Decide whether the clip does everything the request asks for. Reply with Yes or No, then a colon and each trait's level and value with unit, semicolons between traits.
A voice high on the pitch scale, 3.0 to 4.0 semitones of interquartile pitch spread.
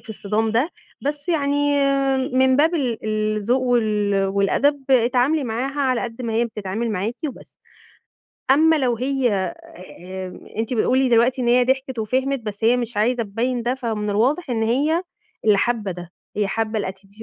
Yes: high, 235 Hz; average, 3.6 semitones